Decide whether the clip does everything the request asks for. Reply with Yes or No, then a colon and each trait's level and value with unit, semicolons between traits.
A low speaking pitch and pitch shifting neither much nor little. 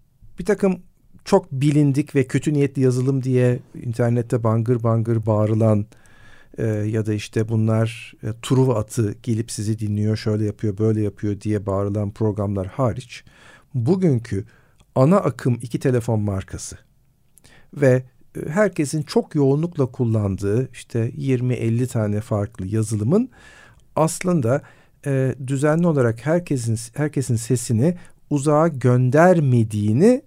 Yes: low, 125 Hz; average, 4.5 semitones